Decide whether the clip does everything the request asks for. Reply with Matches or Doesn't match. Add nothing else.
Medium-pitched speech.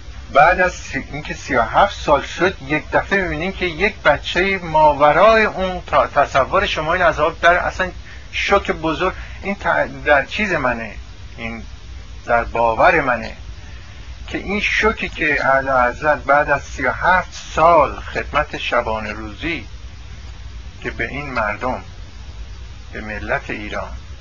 Doesn't match